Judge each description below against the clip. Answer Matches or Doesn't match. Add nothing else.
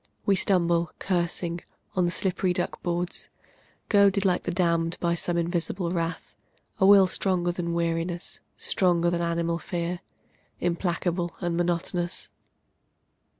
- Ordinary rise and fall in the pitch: Doesn't match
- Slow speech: Matches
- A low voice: Doesn't match